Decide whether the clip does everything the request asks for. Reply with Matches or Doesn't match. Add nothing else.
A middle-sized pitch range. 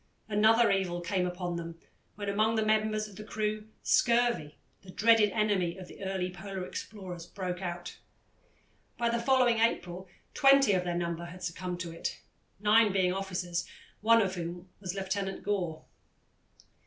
Matches